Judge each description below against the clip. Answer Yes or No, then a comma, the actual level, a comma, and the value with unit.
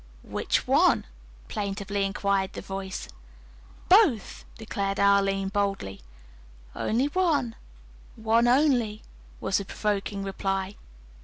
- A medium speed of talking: No, slow, 95 wpm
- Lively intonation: No, average, 2.7 semitones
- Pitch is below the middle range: No, high, 200 Hz